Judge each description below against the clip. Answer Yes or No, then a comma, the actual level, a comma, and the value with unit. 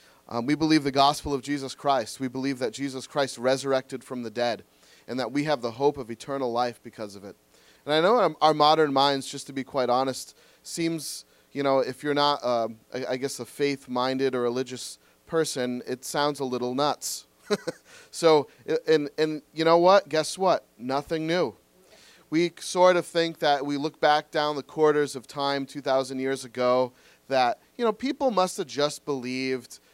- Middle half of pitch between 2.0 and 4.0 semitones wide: Yes, average, 3.2 semitones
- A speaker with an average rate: Yes, average, 190 wpm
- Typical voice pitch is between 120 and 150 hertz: Yes, medium, 140 Hz